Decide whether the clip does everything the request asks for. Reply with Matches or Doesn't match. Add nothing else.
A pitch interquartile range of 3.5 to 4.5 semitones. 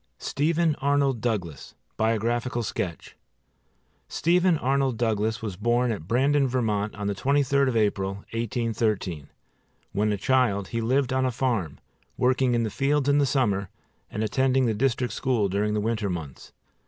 Matches